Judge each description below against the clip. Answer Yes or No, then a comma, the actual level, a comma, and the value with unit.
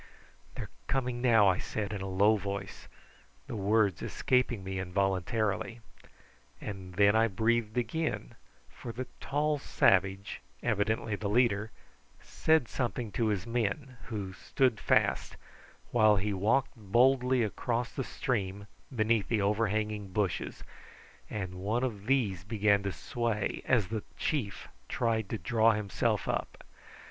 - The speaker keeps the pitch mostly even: No, average, 3.2 semitones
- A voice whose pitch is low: Yes, low, 110 Hz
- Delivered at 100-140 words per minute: Yes, slow, 135 wpm